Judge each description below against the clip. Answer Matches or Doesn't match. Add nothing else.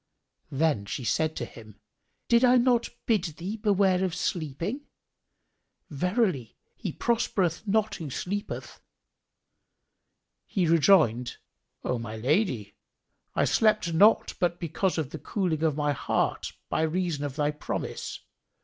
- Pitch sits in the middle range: Matches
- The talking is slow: Matches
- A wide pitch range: Matches